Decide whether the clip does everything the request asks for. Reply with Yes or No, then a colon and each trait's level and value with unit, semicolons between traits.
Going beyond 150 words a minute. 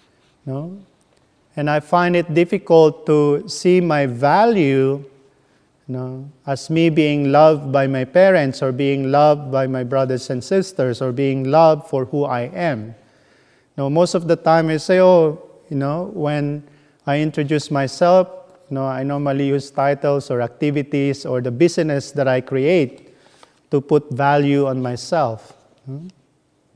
Yes: average, 160 wpm